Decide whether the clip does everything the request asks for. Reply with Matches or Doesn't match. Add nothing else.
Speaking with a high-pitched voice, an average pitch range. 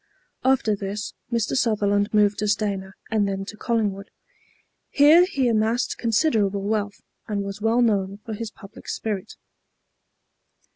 Doesn't match